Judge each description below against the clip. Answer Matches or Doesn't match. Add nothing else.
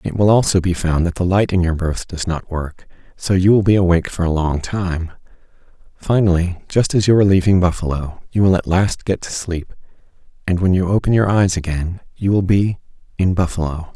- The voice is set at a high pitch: Doesn't match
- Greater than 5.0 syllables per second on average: Matches